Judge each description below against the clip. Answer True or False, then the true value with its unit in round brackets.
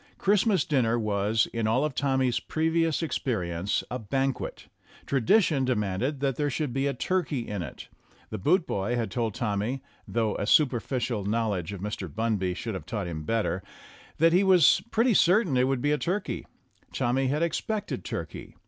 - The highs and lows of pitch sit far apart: True (6.1 semitones)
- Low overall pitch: True (125 Hz)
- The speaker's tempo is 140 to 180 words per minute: True (165 wpm)